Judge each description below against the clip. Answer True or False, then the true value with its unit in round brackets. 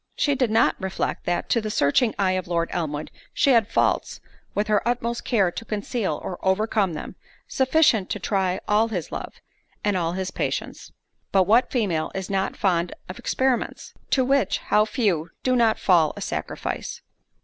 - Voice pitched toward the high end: True (205 Hz)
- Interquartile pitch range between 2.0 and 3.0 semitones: False (4.3 semitones)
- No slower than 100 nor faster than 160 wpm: False (175 wpm)